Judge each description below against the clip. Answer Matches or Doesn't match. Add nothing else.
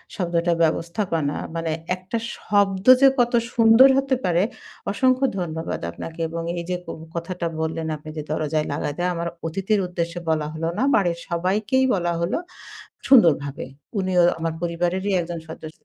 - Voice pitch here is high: Doesn't match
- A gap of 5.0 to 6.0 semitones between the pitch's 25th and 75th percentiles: Doesn't match